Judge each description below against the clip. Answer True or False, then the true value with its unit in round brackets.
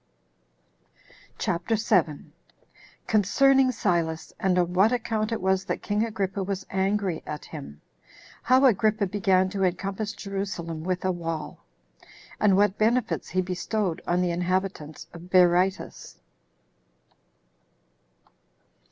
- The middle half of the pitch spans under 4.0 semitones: True (3.0 semitones)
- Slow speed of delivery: True (115 wpm)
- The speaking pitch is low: False (190 Hz)